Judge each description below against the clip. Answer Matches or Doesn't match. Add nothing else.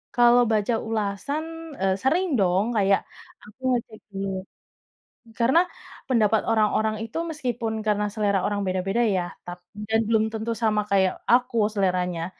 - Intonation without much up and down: Doesn't match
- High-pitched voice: Matches